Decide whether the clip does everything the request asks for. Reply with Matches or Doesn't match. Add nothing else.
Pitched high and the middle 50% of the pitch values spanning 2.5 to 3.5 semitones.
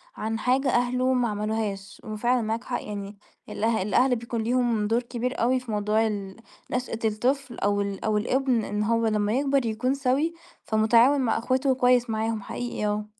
Matches